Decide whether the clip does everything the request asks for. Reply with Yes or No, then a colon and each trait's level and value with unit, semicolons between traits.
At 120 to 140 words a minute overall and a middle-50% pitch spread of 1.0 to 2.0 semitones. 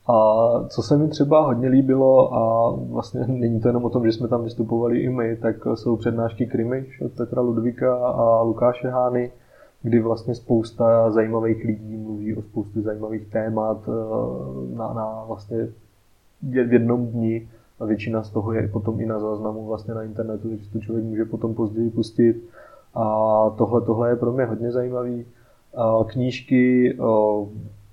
No: average, 160 wpm; narrow, 1.6 semitones